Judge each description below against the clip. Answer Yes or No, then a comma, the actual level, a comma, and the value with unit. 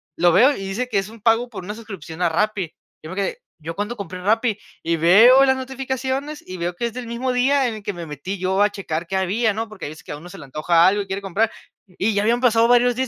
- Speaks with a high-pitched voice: Yes, high, 205 Hz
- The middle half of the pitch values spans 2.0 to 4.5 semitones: No, average, 4.9 semitones